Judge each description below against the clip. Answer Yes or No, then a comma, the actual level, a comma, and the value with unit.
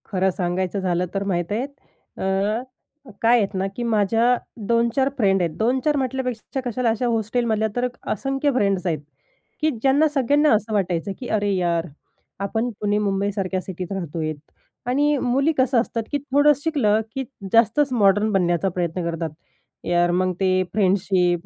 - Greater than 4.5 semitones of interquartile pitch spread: Yes, average, 5.1 semitones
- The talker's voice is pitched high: Yes, high, 210 Hz